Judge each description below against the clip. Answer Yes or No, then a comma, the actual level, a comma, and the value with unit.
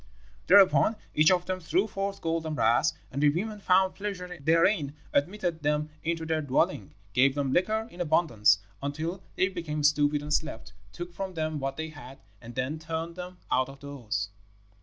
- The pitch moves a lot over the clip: No, average, 4.1 semitones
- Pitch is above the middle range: No, medium, 160 Hz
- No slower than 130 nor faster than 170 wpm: No, average, 180 wpm